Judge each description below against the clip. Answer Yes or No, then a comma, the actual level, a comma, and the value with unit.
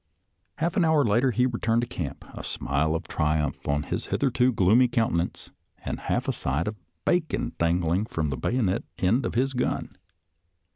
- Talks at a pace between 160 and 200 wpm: Yes, average, 175 wpm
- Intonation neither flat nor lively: No, wide, 7.4 semitones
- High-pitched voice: No, low, 110 Hz